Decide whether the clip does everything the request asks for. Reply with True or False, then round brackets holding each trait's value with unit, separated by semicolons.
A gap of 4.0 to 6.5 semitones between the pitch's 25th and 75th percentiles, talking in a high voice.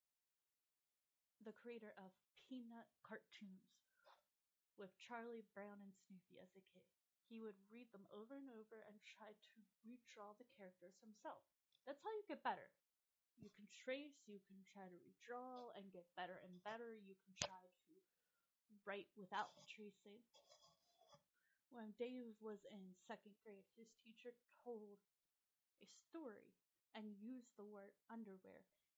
False (3.4 semitones; 215 Hz)